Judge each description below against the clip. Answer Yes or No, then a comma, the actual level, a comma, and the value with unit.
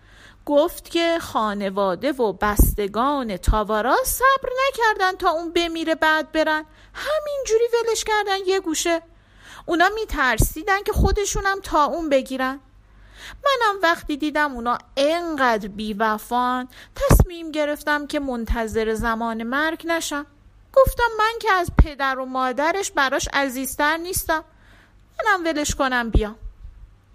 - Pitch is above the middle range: Yes, very high, 300 Hz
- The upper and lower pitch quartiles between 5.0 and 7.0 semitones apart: Yes, wide, 5.5 semitones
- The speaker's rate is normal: Yes, average, 115 wpm